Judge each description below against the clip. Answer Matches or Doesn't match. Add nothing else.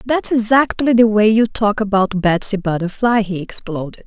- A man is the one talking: Doesn't match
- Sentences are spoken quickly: Doesn't match